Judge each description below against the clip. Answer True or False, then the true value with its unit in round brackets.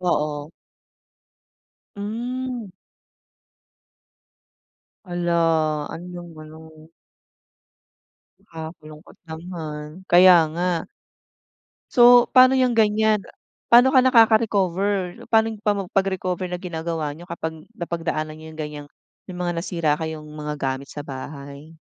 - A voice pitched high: False (175 Hz)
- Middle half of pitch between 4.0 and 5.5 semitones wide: True (4.8 semitones)